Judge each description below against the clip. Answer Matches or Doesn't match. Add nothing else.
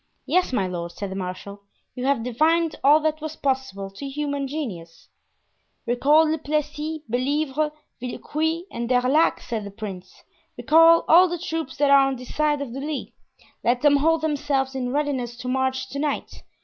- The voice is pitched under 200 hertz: Doesn't match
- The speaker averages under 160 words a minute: Doesn't match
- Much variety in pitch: Doesn't match